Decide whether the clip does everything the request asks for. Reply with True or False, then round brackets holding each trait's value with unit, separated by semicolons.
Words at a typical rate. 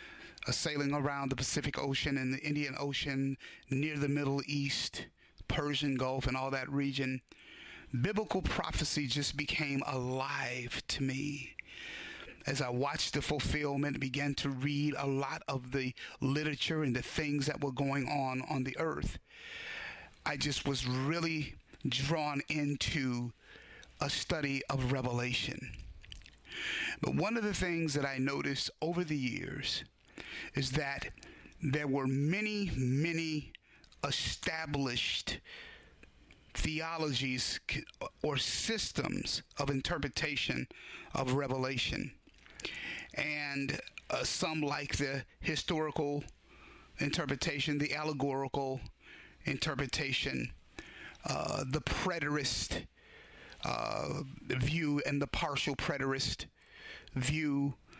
False (110 wpm)